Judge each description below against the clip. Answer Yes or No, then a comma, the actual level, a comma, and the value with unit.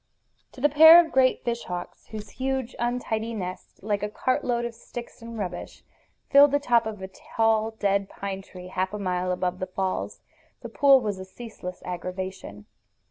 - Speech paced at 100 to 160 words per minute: No, average, 185 wpm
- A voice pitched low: No, high, 215 Hz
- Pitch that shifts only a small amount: No, average, 4.4 semitones